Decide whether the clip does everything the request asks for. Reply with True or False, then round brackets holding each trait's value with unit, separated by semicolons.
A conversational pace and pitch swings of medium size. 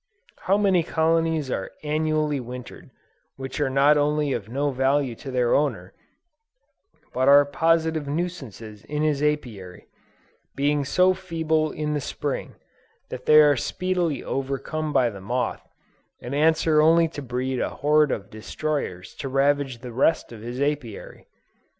True (145 wpm; 3.3 semitones)